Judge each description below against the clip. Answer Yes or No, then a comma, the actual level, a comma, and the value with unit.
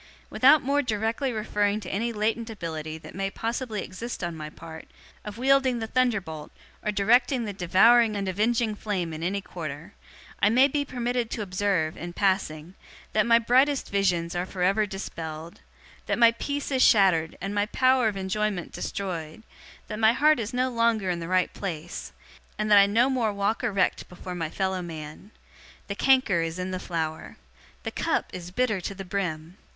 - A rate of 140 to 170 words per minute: No, average, 180 wpm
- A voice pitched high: Yes, high, 200 Hz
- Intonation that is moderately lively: Yes, average, 4.6 semitones